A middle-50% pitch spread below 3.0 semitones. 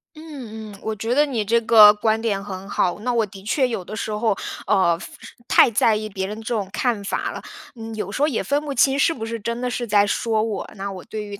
Yes: narrow, 2.4 semitones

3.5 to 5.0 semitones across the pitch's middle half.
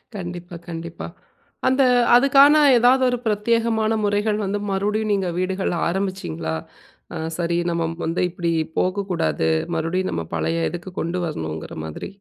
Yes: average, 4.2 semitones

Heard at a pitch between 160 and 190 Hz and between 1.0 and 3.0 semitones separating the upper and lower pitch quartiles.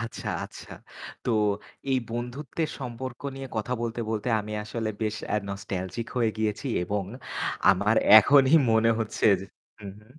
No: low, 115 Hz; average, 2.7 semitones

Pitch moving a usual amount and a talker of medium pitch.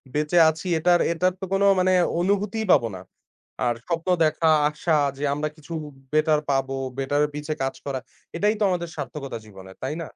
Yes: average, 4.0 semitones; medium, 155 Hz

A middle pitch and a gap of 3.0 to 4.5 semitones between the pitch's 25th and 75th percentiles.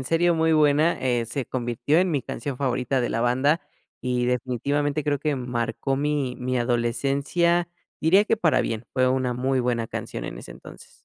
No: low, 130 Hz; average, 3.4 semitones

